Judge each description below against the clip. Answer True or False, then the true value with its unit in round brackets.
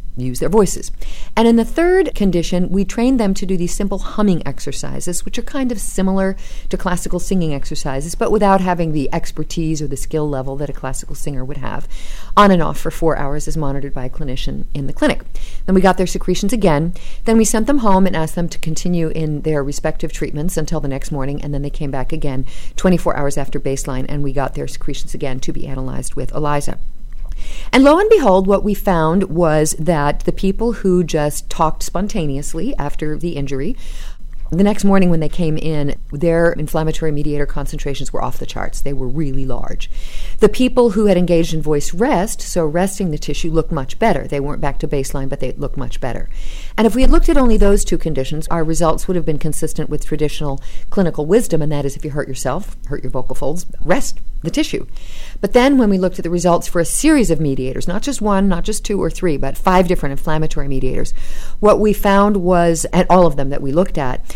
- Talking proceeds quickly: True (220 wpm)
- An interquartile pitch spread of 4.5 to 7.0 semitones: True (5.0 semitones)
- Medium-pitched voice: True (160 Hz)